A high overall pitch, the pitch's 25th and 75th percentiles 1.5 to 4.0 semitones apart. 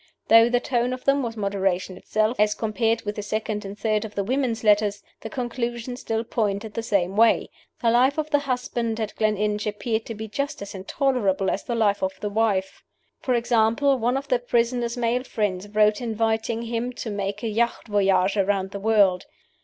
Yes: high, 220 Hz; narrow, 2.6 semitones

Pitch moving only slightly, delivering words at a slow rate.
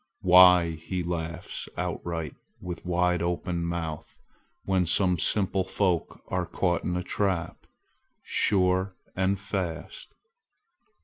Yes: narrow, 1.6 semitones; slow, 110 wpm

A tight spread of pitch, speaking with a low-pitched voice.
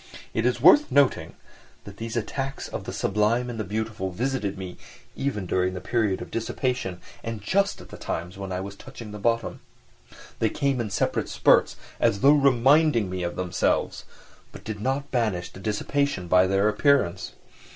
No: wide, 5.6 semitones; low, 110 Hz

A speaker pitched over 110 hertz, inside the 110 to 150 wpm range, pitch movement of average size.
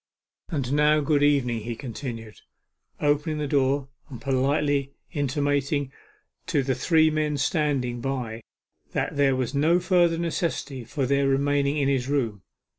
No: medium, 140 Hz; average, 140 wpm; narrow, 2.2 semitones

